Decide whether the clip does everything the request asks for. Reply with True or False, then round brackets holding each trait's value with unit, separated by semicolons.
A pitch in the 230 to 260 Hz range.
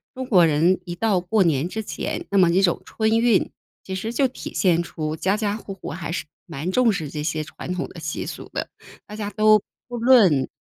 False (190 Hz)